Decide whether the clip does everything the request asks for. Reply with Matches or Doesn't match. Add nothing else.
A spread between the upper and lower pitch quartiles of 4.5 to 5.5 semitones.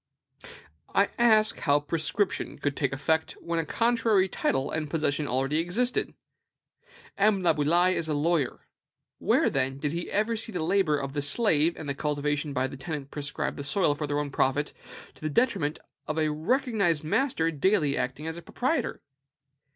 Matches